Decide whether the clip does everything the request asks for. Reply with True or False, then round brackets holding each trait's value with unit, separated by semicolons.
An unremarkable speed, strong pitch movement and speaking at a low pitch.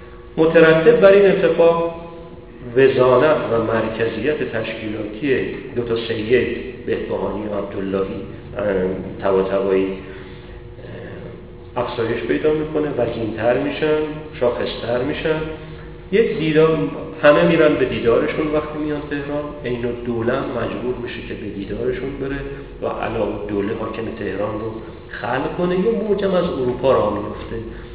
True (115 wpm; 6.0 semitones; 120 Hz)